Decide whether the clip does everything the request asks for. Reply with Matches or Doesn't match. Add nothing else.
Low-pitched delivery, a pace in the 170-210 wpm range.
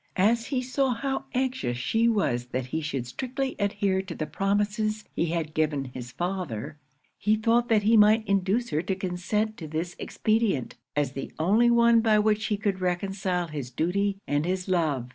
Doesn't match